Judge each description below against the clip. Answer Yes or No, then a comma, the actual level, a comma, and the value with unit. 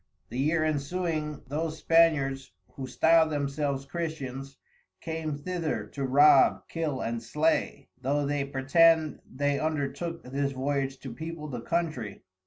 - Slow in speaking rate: Yes, slow, 130 wpm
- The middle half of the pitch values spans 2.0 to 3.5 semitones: Yes, average, 2.9 semitones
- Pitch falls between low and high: Yes, medium, 145 Hz